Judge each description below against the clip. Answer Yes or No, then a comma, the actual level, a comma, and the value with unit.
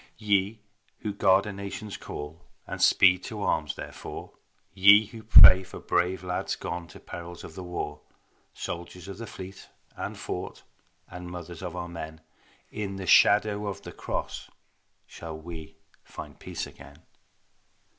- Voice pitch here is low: Yes, very low, 95 Hz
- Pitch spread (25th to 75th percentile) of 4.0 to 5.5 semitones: No, average, 2.8 semitones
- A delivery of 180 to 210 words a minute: No, average, 150 wpm